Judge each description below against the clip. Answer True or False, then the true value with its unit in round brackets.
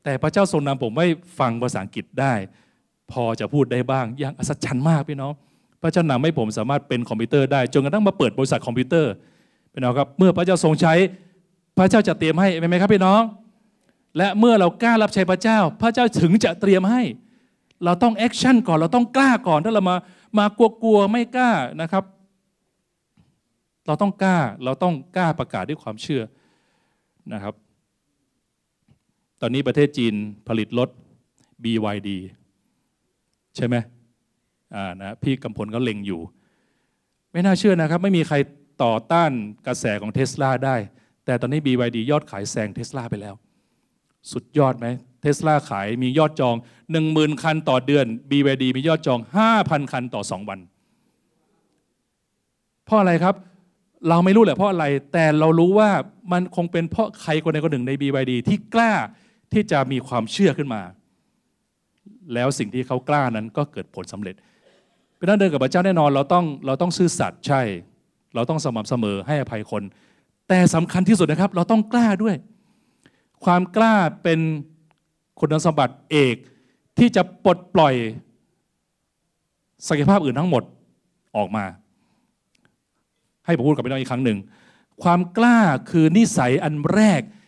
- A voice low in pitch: False (155 Hz)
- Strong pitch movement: True (7.0 semitones)